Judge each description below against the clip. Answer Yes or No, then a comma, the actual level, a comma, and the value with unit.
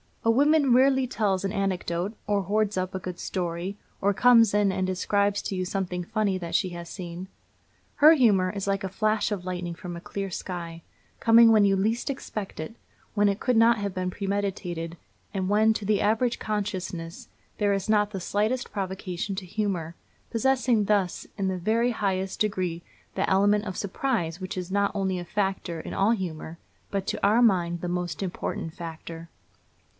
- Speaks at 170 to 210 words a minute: Yes, average, 185 wpm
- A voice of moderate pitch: No, high, 195 Hz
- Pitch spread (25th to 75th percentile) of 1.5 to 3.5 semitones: Yes, average, 2.8 semitones